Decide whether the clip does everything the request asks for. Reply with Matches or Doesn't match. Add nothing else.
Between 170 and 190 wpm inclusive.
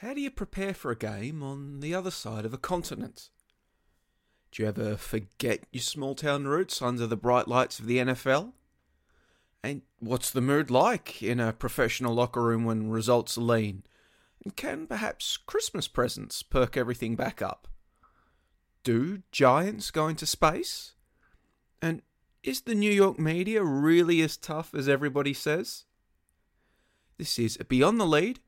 Doesn't match